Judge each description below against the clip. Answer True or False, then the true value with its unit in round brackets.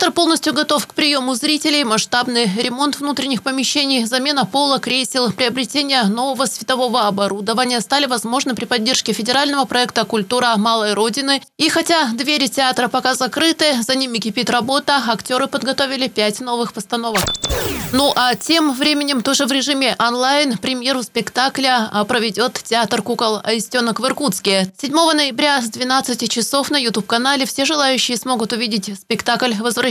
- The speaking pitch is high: True (255 Hz)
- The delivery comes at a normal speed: True (140 wpm)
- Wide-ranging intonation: False (3.1 semitones)